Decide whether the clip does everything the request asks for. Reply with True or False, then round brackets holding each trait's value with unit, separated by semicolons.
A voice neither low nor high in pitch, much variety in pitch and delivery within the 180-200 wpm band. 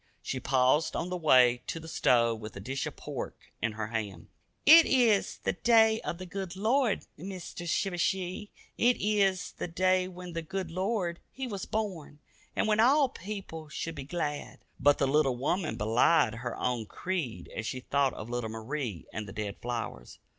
True (165 Hz; 7.7 semitones; 185 wpm)